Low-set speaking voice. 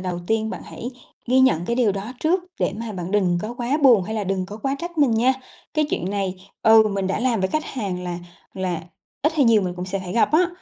No: high, 215 Hz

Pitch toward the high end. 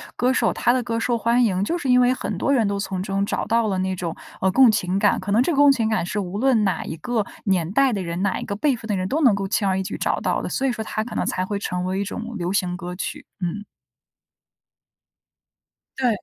Yes: high, 210 Hz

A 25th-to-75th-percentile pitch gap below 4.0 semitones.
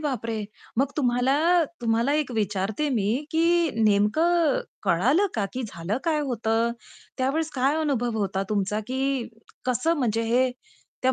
No: average, 4.8 semitones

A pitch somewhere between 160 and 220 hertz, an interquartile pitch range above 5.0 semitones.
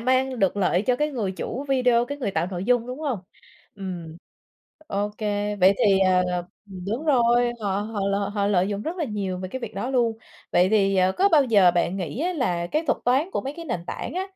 Yes: high, 210 Hz; wide, 5.4 semitones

